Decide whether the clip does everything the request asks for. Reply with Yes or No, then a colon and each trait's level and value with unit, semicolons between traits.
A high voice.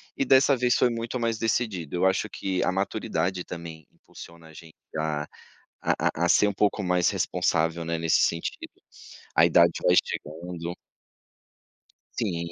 No: very low, 90 Hz